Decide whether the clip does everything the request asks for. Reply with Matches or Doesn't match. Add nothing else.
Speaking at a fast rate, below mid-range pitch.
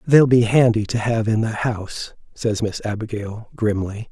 Doesn't match